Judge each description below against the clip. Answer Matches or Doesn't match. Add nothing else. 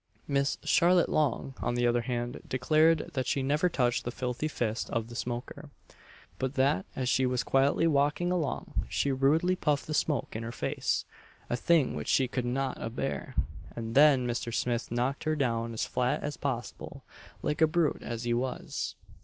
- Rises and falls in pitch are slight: Doesn't match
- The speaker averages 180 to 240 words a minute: Matches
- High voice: Doesn't match